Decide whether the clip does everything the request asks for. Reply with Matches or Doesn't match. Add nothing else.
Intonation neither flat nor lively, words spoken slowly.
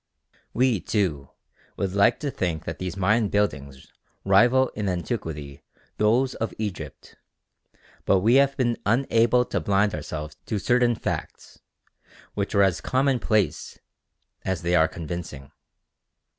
Doesn't match